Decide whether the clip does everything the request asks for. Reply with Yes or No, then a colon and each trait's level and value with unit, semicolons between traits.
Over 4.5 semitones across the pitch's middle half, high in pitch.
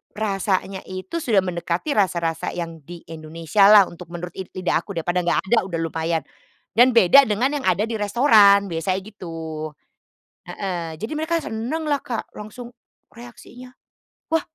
Yes: average, 5.2 semitones; high, 195 Hz